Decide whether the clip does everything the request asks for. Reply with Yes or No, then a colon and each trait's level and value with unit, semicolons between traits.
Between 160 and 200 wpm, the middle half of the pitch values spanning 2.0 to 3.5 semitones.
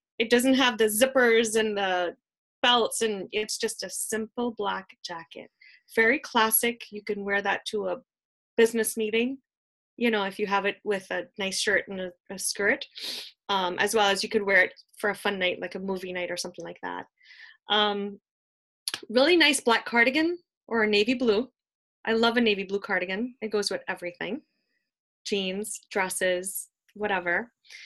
Yes: average, 170 wpm; average, 3.2 semitones